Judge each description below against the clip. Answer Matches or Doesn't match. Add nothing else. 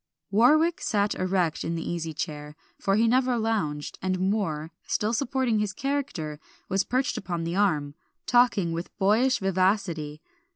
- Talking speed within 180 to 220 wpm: Doesn't match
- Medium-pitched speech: Doesn't match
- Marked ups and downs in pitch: Matches